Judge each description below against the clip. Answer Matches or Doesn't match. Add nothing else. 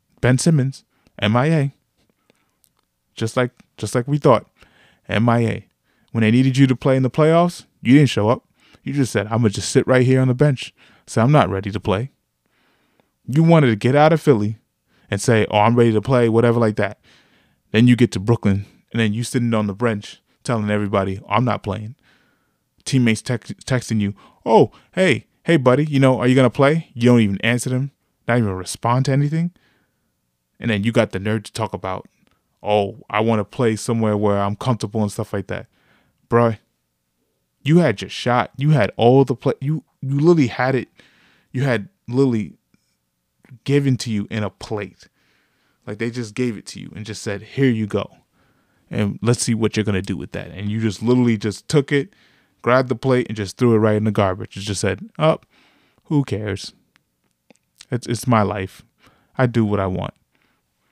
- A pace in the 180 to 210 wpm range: Matches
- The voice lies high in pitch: Doesn't match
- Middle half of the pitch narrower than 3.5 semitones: Doesn't match